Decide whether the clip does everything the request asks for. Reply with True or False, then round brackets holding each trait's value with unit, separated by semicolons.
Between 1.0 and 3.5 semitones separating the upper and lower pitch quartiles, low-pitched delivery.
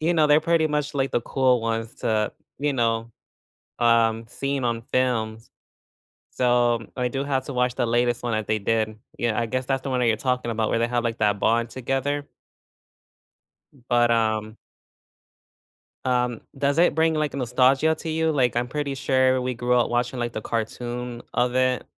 True (2.7 semitones; 125 Hz)